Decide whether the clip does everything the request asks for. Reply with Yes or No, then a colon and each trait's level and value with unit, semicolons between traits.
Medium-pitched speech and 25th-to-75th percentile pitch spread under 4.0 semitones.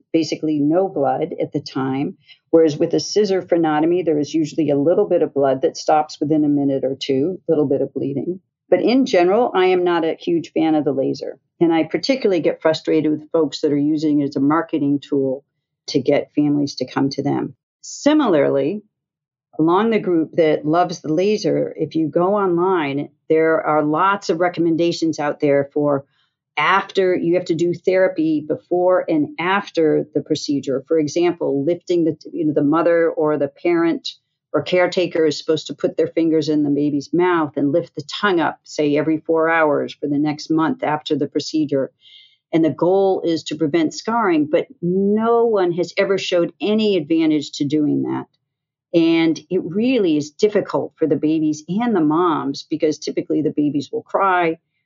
Yes: medium, 160 Hz; average, 3.3 semitones